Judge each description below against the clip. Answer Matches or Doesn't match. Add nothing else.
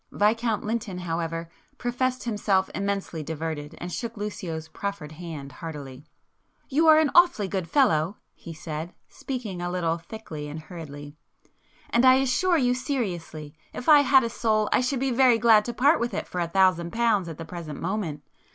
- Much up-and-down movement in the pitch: Matches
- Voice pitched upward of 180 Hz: Matches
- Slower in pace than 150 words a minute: Doesn't match